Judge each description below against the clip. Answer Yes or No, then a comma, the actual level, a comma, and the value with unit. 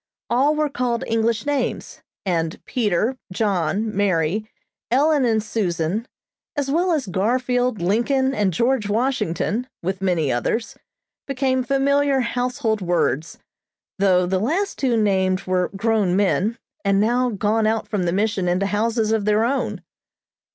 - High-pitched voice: Yes, high, 220 Hz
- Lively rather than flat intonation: No, average, 4.9 semitones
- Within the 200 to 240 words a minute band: No, average, 140 wpm